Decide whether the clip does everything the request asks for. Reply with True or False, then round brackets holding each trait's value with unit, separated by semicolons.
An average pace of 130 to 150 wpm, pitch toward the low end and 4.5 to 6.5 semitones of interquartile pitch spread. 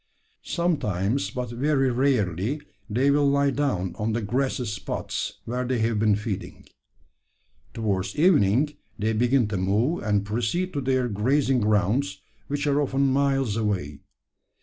True (140 wpm; 120 Hz; 4.9 semitones)